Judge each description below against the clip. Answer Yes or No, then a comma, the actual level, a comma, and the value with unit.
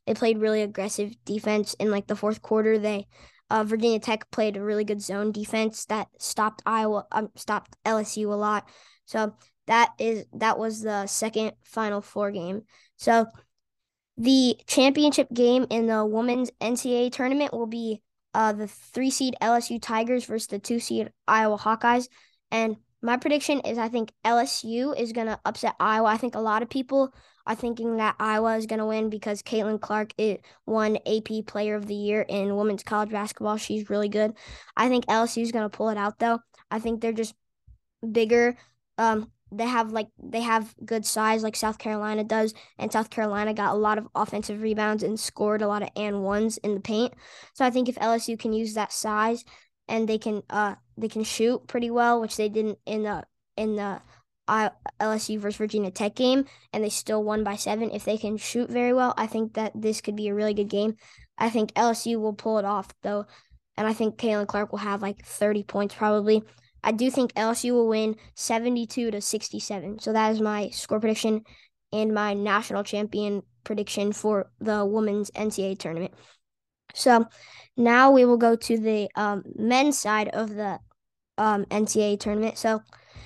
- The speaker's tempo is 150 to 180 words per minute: No, average, 190 wpm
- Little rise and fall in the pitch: Yes, narrow, 1.4 semitones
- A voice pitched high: Yes, high, 220 Hz